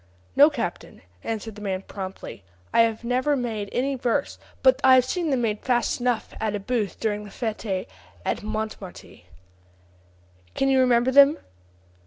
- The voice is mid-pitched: No, high, 230 Hz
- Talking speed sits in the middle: Yes, average, 160 wpm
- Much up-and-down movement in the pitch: No, average, 3.8 semitones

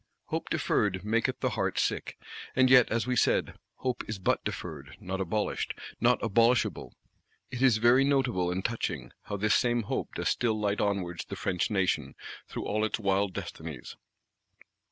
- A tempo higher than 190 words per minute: No, average, 165 wpm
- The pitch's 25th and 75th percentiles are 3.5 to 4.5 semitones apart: Yes, average, 3.8 semitones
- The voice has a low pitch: Yes, low, 110 Hz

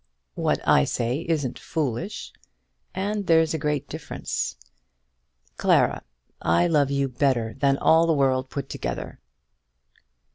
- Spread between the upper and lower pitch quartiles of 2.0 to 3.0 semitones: No, average, 3.8 semitones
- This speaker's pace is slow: Yes, slow, 120 wpm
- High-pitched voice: No, medium, 140 Hz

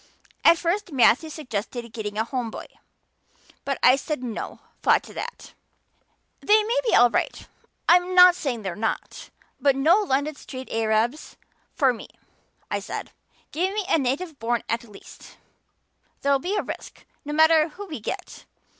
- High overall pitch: Yes, very high, 280 Hz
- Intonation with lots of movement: Yes, wide, 6.6 semitones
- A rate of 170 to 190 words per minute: No, average, 160 wpm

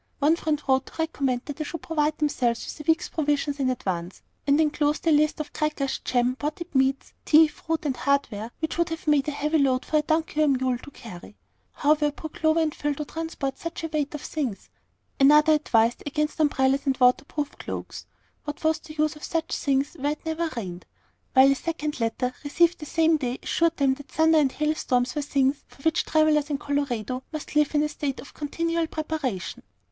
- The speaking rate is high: Yes, fast, 210 wpm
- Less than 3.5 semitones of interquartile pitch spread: Yes, average, 2.7 semitones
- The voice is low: No, very high, 295 Hz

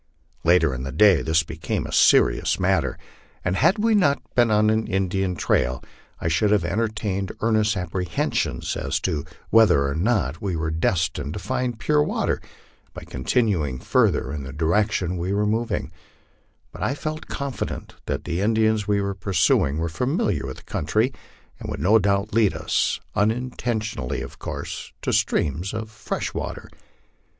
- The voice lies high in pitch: No, low, 100 Hz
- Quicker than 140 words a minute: Yes, average, 165 wpm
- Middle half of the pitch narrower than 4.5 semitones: No, average, 5.2 semitones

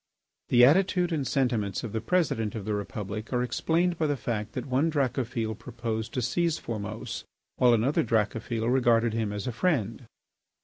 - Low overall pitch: Yes, low, 120 Hz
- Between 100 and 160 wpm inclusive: No, average, 170 wpm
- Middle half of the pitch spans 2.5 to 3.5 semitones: No, average, 4.0 semitones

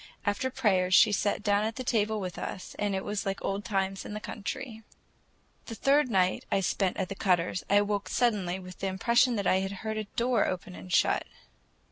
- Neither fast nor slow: No, fast, 210 wpm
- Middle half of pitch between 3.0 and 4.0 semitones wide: No, narrow, 2.6 semitones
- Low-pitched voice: No, high, 205 Hz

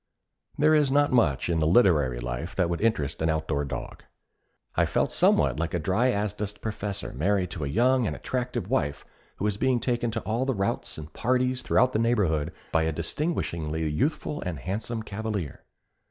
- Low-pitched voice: Yes, low, 100 Hz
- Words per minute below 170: No, average, 185 wpm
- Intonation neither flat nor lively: No, wide, 7.2 semitones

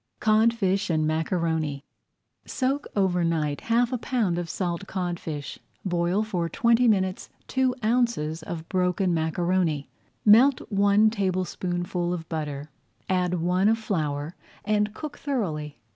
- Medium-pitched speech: Yes, medium, 180 Hz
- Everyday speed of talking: No, slow, 125 wpm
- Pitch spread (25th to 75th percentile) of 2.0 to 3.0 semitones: No, average, 4.8 semitones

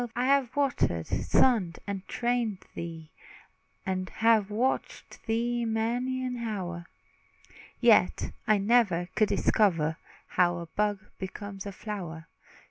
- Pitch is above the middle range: Yes, high, 210 Hz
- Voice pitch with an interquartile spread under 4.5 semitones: No, average, 4.8 semitones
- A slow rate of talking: Yes, slow, 120 wpm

